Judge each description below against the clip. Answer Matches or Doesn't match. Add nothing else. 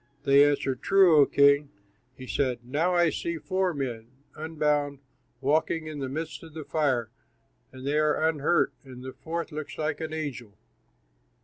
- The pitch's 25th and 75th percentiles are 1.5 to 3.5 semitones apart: Matches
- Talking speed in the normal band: Matches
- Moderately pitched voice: Matches